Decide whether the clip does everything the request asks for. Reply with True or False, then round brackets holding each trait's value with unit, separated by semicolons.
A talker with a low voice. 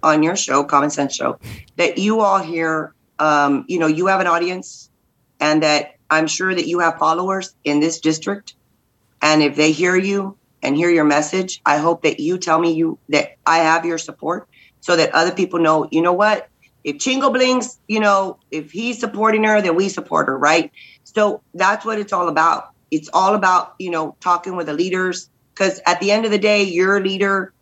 False (175 Hz)